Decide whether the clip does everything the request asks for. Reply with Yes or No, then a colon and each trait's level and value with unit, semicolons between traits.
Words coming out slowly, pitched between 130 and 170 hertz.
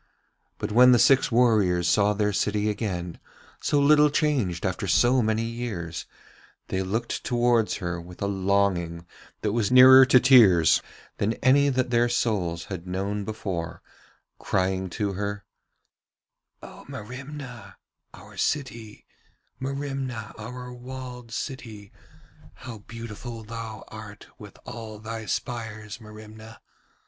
No: slow, 125 wpm; low, 110 Hz